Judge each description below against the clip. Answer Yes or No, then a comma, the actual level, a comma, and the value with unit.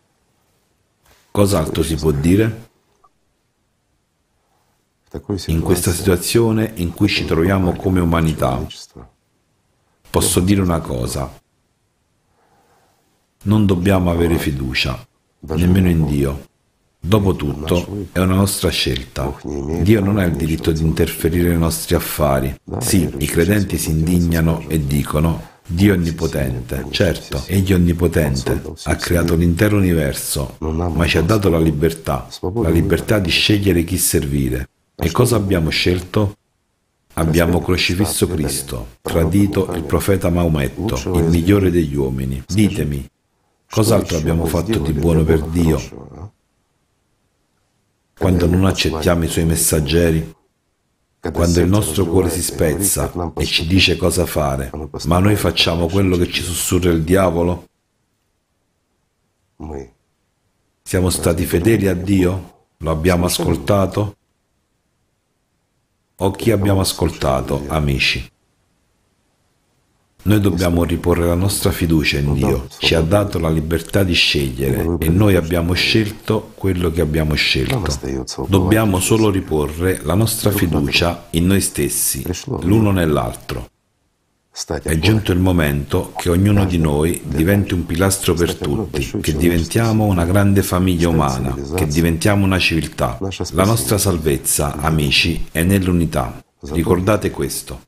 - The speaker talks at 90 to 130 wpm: Yes, average, 120 wpm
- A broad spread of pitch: No, average, 3.4 semitones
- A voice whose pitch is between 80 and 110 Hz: Yes, very low, 85 Hz